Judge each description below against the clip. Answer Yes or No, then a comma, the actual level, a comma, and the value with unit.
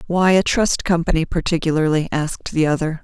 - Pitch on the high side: No, medium, 165 Hz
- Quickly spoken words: No, average, 160 wpm